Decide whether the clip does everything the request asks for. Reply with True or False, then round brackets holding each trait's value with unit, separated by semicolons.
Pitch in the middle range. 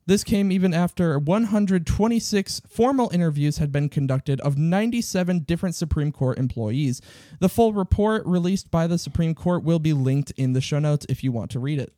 True (165 Hz)